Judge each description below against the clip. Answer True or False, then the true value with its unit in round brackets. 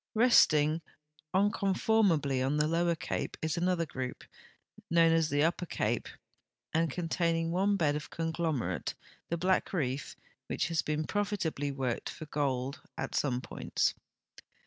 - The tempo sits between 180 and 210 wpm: False (140 wpm)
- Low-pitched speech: False (160 Hz)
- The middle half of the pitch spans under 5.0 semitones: True (3.2 semitones)